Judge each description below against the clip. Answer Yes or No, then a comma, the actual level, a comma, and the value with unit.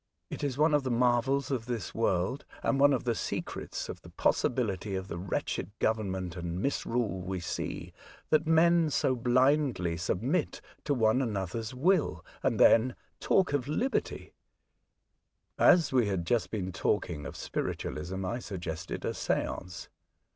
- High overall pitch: No, low, 120 Hz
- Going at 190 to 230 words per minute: No, average, 150 wpm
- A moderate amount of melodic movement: No, wide, 6.7 semitones